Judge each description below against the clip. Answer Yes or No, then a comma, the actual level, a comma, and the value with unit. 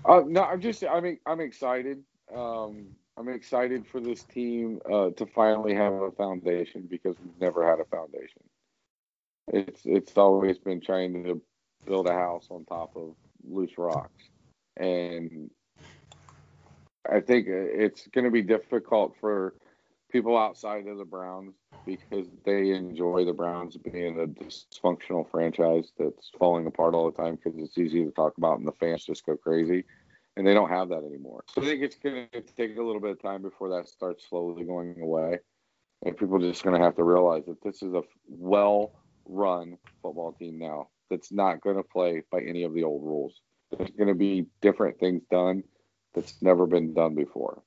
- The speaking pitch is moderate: No, very low, 95 Hz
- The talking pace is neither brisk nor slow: Yes, average, 185 wpm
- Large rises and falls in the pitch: No, average, 3.9 semitones